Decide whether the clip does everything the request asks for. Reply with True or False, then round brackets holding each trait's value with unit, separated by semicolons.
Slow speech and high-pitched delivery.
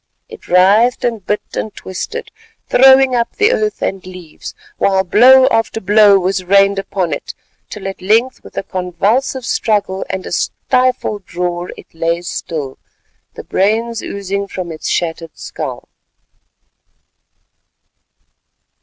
True (125 wpm; 200 Hz)